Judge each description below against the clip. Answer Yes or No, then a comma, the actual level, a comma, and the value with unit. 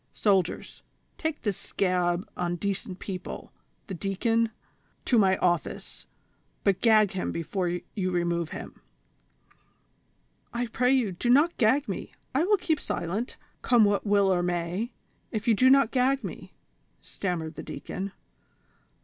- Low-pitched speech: No, high, 200 Hz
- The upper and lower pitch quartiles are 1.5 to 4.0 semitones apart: No, average, 5.1 semitones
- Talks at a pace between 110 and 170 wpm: Yes, average, 155 wpm